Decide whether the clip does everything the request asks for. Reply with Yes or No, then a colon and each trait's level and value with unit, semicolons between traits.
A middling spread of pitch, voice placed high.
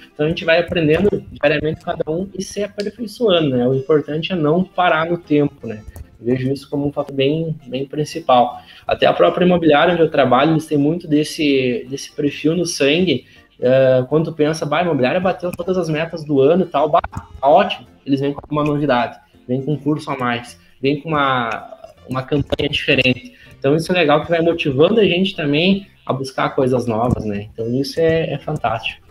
No: average, 3.7 semitones; medium, 150 Hz